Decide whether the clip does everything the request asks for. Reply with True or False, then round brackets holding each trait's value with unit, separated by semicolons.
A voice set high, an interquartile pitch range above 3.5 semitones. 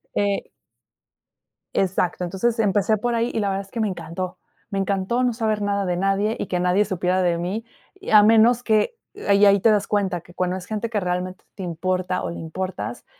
False (195 Hz; 2.9 semitones)